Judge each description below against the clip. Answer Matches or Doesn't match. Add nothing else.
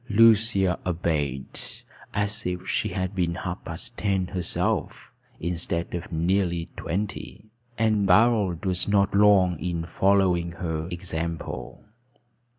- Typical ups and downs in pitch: Matches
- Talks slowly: Matches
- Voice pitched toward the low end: Matches